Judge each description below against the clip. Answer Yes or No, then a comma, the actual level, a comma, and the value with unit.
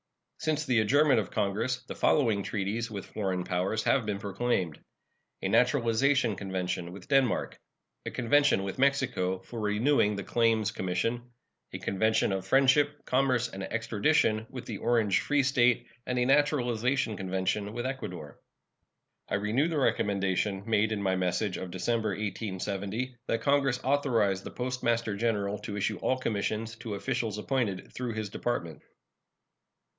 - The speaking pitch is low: Yes, low, 110 Hz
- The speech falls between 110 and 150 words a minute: Yes, average, 145 wpm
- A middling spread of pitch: Yes, average, 4.3 semitones